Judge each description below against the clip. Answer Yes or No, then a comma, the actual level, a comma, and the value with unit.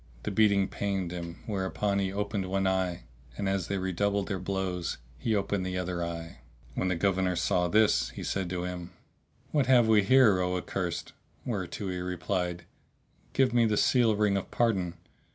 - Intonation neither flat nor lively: No, narrow, 2.3 semitones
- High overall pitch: No, very low, 95 Hz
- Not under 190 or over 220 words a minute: No, average, 175 wpm